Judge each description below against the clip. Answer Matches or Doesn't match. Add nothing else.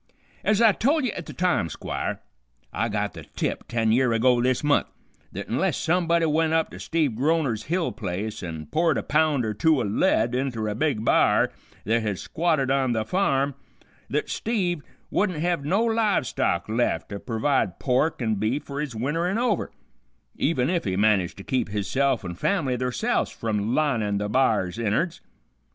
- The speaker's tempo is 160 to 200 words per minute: Matches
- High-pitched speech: Doesn't match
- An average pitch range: Doesn't match